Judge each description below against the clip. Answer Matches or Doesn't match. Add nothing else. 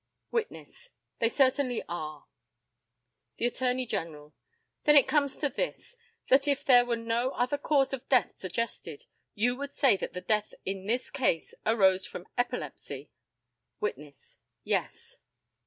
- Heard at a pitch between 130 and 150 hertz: Doesn't match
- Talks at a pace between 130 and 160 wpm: Matches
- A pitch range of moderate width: Doesn't match